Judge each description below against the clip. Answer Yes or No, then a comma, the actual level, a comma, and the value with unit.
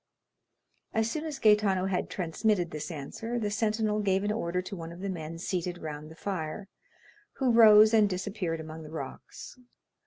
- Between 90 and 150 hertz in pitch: No, high, 195 Hz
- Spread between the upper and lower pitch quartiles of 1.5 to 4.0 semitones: No, average, 4.4 semitones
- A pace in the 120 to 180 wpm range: Yes, average, 175 wpm